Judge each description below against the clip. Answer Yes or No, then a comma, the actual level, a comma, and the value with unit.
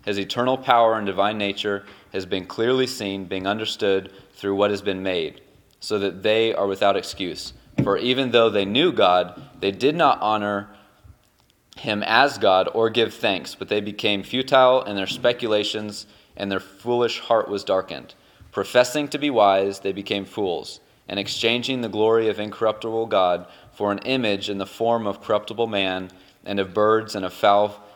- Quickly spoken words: No, average, 175 wpm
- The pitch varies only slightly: Yes, narrow, 2.3 semitones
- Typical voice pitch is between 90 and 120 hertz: Yes, low, 105 Hz